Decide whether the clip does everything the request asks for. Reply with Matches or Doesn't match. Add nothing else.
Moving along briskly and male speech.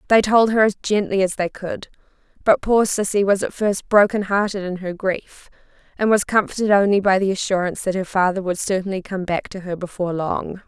Doesn't match